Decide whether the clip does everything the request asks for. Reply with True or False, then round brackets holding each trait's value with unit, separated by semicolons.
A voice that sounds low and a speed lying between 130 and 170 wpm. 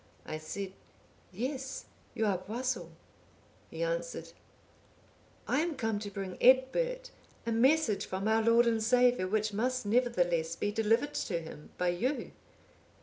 False (220 Hz; 140 wpm)